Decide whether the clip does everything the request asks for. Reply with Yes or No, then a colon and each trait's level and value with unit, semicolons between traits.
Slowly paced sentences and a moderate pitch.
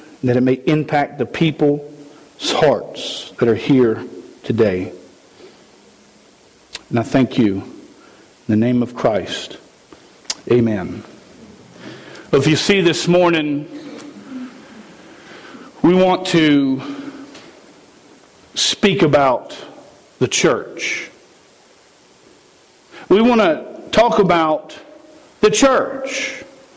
Yes: slow, 90 wpm; medium, 155 Hz